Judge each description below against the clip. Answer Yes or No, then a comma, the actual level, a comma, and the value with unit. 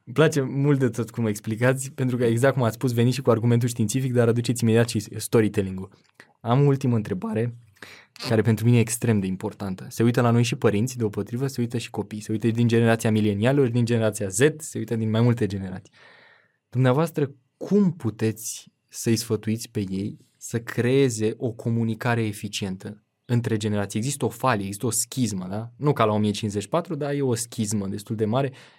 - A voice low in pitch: Yes, low, 115 Hz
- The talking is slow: No, fast, 190 wpm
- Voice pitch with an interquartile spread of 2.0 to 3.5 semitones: Yes, average, 2.9 semitones